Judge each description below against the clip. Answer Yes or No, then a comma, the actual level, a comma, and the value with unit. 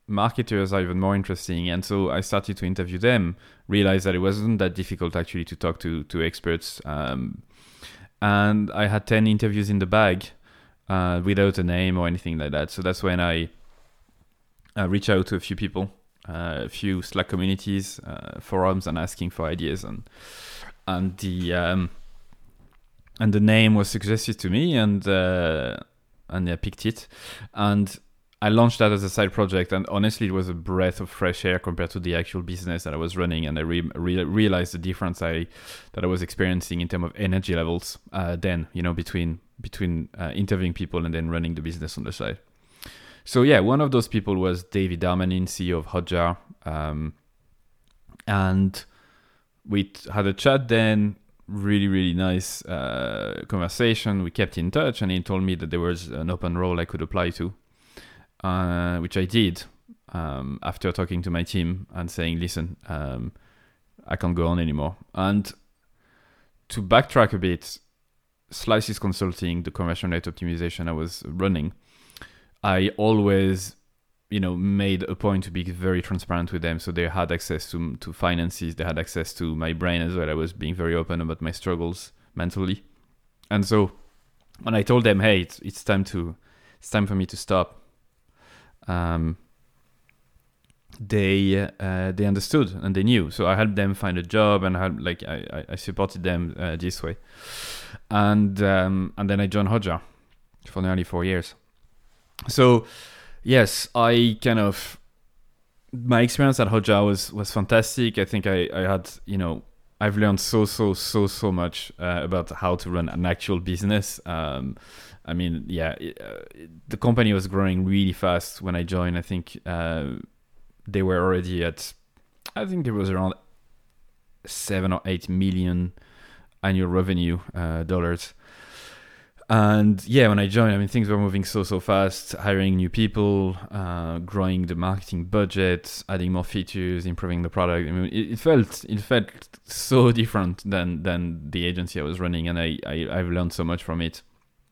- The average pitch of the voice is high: No, very low, 95 Hz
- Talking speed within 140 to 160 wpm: No, average, 180 wpm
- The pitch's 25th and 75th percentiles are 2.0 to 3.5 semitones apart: Yes, average, 2.8 semitones